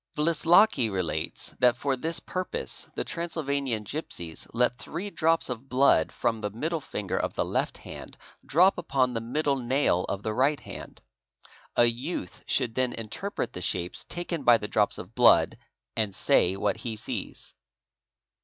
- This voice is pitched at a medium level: No, low, 125 Hz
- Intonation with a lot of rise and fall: Yes, wide, 6.2 semitones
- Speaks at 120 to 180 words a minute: Yes, average, 160 wpm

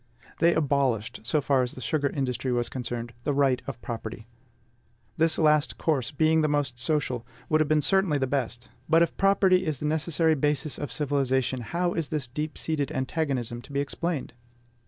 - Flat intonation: No, average, 3.6 semitones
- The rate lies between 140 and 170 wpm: No, average, 180 wpm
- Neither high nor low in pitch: Yes, medium, 145 Hz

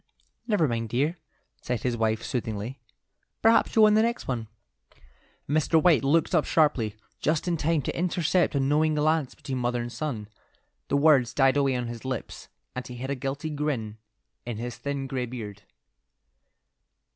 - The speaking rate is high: No, average, 170 wpm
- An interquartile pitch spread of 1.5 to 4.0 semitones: No, average, 4.4 semitones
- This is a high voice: No, low, 135 Hz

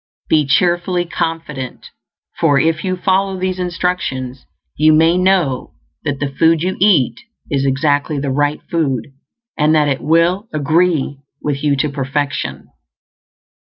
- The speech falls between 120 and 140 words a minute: Yes, slow, 135 wpm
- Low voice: No, medium, 155 Hz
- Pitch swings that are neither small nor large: Yes, average, 3.9 semitones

